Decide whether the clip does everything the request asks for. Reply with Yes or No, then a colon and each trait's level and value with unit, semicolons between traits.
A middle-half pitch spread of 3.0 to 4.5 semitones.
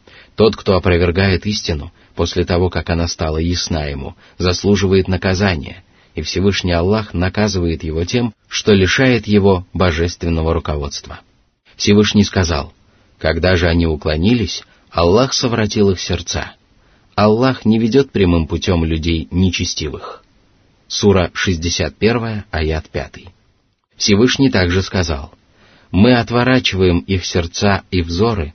Yes: average, 3.3 semitones